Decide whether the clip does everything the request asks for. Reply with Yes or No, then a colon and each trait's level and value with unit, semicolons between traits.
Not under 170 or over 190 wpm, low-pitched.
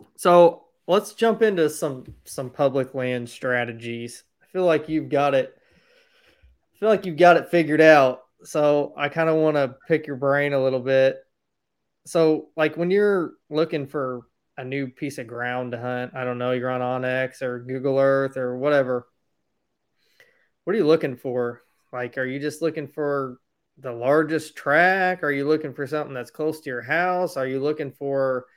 No: average, 185 wpm; medium, 145 Hz